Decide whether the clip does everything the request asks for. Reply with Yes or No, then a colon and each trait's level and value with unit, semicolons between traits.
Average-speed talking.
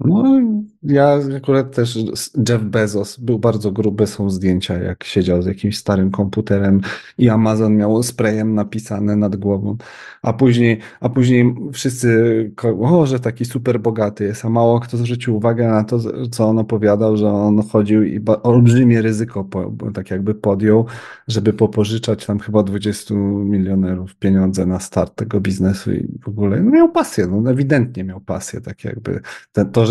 No: fast, 165 wpm